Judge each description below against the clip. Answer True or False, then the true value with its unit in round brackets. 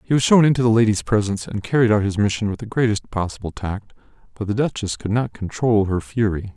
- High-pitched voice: False (110 Hz)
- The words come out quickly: True (230 wpm)